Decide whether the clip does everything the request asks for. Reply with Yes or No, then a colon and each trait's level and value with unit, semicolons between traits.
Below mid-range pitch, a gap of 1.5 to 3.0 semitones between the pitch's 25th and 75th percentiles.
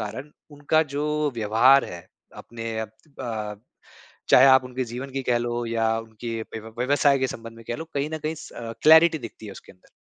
No: low, 120 Hz; average, 4.0 semitones